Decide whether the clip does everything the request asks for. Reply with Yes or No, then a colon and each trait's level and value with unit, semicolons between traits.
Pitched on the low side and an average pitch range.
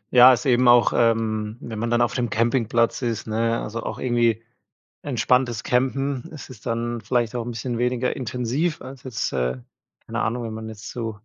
No: low, 120 Hz; narrow, 1.8 semitones